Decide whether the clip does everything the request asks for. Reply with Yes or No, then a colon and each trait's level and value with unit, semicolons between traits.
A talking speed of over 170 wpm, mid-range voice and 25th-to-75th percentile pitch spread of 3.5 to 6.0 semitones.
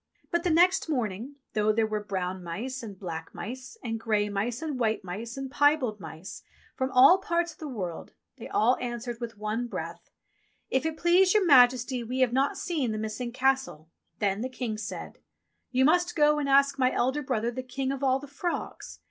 No: average, 200 wpm; very high, 250 Hz; average, 4.4 semitones